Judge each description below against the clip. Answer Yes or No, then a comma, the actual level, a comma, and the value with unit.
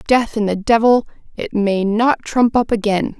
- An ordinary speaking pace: Yes, average, 170 wpm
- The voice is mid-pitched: No, high, 220 Hz